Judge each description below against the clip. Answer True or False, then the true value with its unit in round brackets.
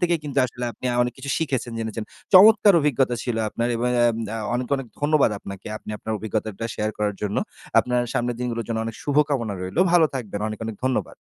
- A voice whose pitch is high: False (120 Hz)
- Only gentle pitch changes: False (4.1 semitones)